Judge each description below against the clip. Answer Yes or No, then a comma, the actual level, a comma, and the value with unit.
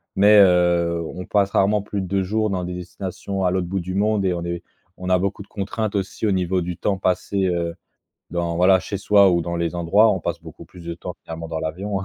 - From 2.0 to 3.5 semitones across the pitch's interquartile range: Yes, narrow, 2.4 semitones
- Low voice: Yes, very low, 90 Hz